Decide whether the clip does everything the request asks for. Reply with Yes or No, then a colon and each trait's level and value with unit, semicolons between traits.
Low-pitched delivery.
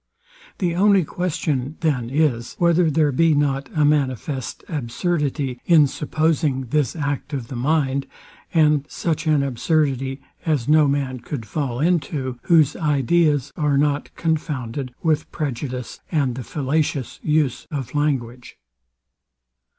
No: medium, 145 Hz